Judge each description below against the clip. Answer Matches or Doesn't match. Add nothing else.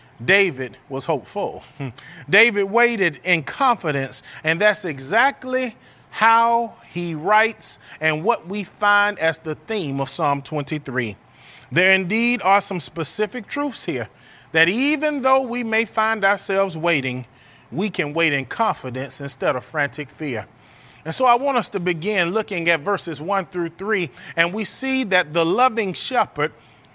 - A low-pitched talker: Doesn't match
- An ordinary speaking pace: Matches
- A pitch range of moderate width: Doesn't match